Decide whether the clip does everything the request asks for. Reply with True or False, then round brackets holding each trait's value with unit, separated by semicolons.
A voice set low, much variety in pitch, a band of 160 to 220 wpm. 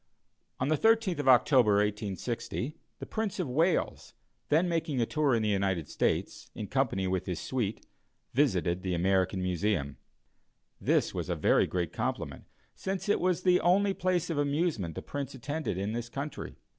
True (125 Hz; 8.9 semitones; 170 wpm)